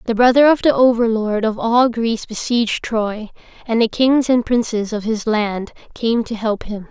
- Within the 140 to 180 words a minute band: No, average, 190 wpm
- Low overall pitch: No, high, 230 Hz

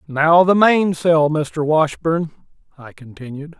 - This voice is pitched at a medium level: Yes, medium, 155 Hz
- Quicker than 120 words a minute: No, slow, 115 wpm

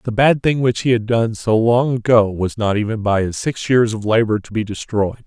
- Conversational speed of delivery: No, fast, 250 wpm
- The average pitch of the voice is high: No, low, 110 Hz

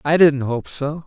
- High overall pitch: No, medium, 145 Hz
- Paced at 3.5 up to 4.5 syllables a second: Yes, 4.1 syllables/s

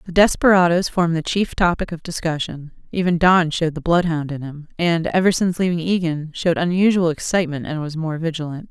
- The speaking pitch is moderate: Yes, medium, 170 Hz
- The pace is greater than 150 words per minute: Yes, average, 185 wpm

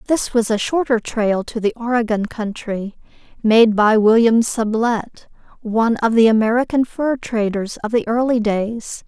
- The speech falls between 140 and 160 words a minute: Yes, average, 150 wpm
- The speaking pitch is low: No, high, 225 Hz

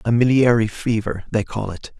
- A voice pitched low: Yes, low, 110 Hz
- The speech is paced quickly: No, average, 180 wpm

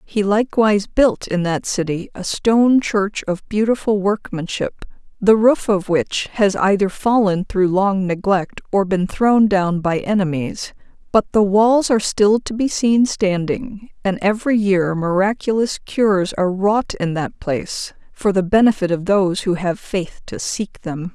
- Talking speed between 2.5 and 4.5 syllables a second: Yes, 4.4 syllables/s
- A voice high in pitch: Yes, high, 200 Hz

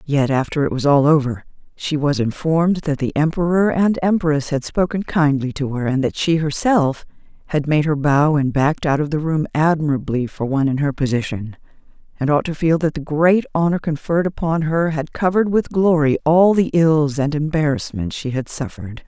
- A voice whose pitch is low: No, medium, 150 Hz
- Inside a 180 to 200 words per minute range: Yes, average, 195 wpm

